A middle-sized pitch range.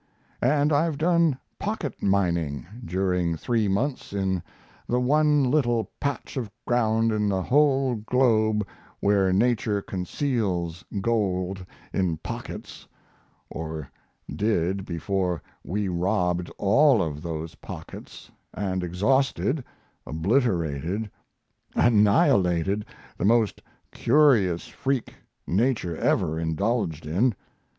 No: wide, 5.7 semitones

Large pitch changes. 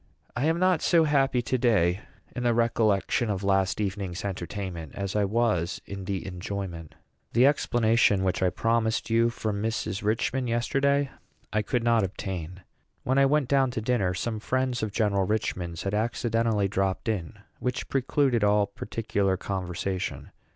No: average, 3.9 semitones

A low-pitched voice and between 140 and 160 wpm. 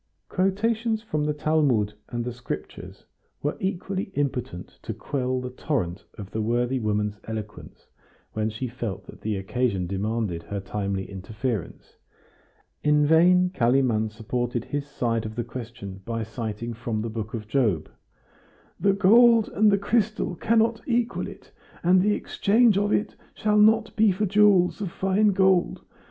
Yes: low, 130 Hz; average, 150 wpm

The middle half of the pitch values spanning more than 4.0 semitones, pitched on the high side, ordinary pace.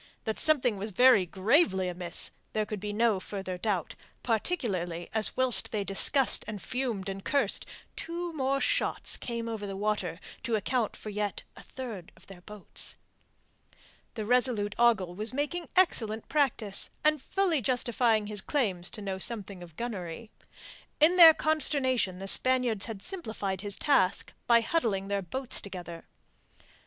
Yes: average, 5.0 semitones; high, 215 Hz; average, 150 wpm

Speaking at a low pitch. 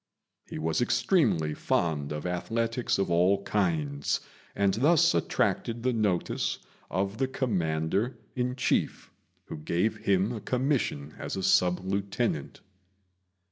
Yes: low, 100 Hz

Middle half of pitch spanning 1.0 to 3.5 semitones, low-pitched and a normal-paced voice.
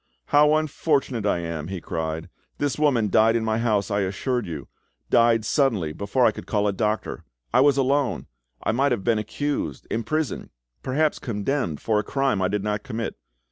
No: average, 5.2 semitones; low, 115 Hz; average, 180 wpm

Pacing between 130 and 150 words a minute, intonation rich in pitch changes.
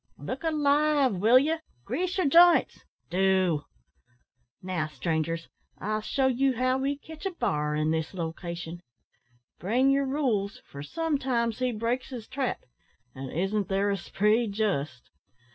Yes: average, 145 wpm; wide, 7.8 semitones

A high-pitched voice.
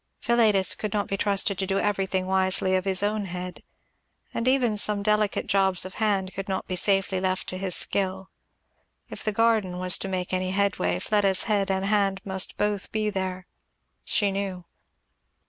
Yes: high, 195 Hz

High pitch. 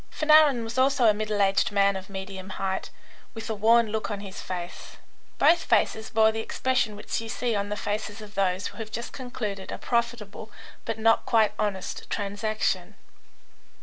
Yes: high, 215 Hz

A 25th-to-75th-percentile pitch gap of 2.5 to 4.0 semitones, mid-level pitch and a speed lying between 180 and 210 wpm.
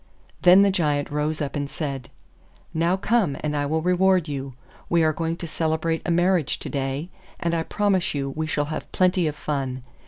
Yes: average, 3.4 semitones; medium, 160 Hz; average, 195 wpm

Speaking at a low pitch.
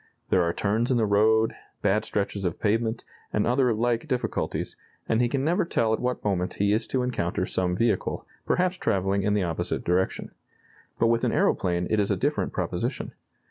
Yes: low, 110 Hz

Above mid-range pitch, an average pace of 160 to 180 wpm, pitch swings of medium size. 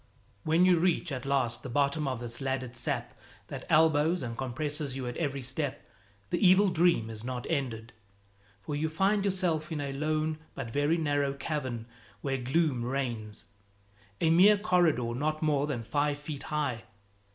No: medium, 145 Hz; average, 165 wpm; average, 3.9 semitones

